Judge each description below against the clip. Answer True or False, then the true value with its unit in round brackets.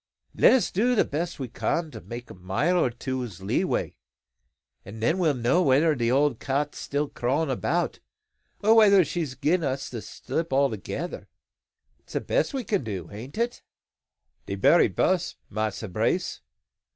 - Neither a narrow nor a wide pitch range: False (6.5 semitones)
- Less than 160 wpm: False (165 wpm)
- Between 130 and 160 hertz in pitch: True (140 Hz)